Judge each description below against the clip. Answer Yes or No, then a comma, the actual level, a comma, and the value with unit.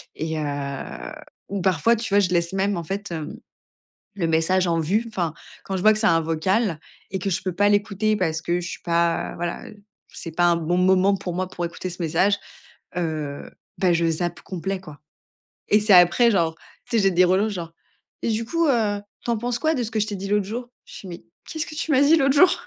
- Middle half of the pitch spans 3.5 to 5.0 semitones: Yes, average, 4.0 semitones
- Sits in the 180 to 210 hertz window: Yes, medium, 185 Hz